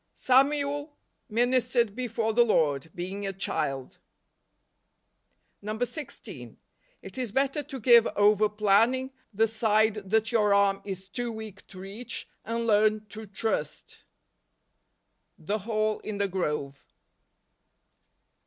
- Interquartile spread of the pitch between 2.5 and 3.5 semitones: Yes, average, 3.1 semitones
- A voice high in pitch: Yes, high, 215 Hz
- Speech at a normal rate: No, slow, 115 wpm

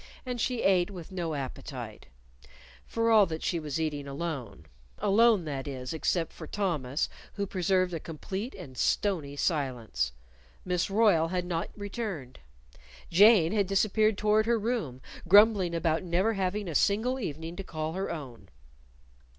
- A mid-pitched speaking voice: Yes, medium, 180 Hz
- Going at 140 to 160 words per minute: Yes, average, 150 wpm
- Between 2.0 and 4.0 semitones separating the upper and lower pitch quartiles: No, average, 4.8 semitones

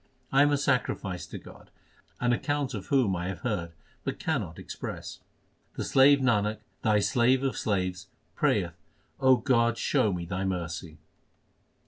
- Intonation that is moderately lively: No, wide, 6.1 semitones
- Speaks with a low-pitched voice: Yes, low, 110 Hz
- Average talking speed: Yes, average, 150 wpm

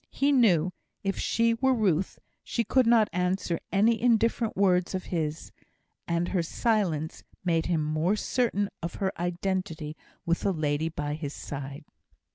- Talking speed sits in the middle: Yes, average, 150 wpm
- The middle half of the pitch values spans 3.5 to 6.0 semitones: Yes, average, 5.1 semitones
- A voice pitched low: No, medium, 180 Hz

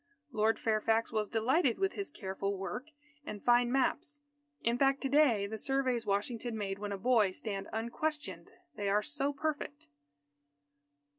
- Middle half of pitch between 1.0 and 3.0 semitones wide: No, average, 4.7 semitones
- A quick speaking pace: No, average, 150 wpm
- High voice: Yes, high, 235 Hz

